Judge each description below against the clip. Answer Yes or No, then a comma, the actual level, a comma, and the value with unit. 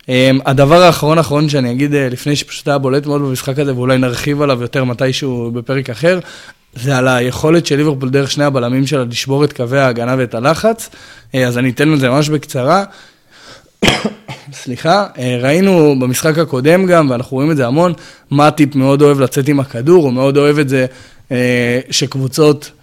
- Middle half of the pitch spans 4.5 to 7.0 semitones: No, average, 2.7 semitones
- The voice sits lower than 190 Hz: Yes, medium, 140 Hz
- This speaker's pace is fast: Yes, fast, 180 wpm